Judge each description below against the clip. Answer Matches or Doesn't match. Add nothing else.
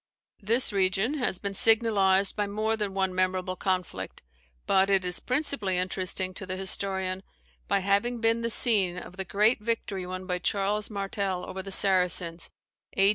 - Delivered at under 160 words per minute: Doesn't match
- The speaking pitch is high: Matches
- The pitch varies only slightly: Matches